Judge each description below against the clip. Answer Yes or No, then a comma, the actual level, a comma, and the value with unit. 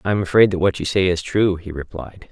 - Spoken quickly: Yes, fast, 285 wpm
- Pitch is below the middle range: Yes, very low, 90 Hz